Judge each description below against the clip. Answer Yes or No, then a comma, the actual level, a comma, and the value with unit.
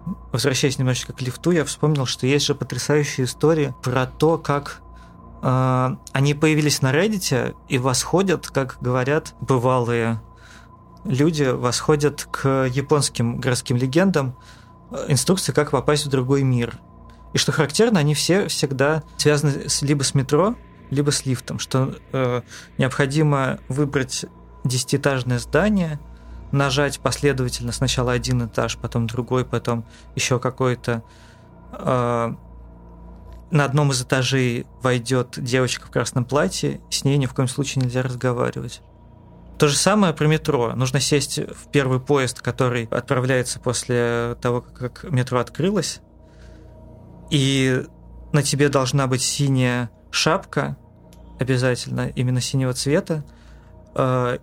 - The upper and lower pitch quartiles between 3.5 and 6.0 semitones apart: No, average, 2.9 semitones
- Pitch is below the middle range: Yes, low, 130 Hz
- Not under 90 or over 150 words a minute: Yes, average, 125 wpm